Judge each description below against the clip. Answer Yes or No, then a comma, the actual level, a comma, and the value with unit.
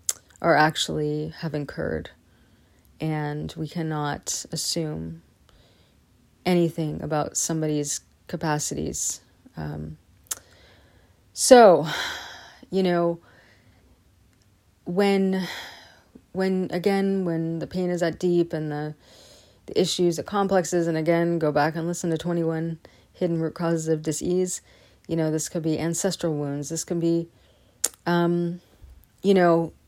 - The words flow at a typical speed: No, slow, 115 wpm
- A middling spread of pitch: No, wide, 8.6 semitones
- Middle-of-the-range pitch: Yes, medium, 160 Hz